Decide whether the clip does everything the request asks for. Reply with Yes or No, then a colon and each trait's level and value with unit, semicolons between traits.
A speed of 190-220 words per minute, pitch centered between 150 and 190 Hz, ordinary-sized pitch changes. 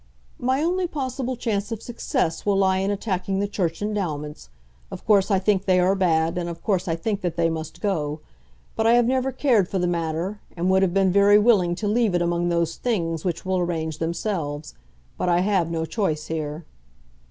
Yes: fast, 205 wpm; medium, 185 Hz; average, 3.8 semitones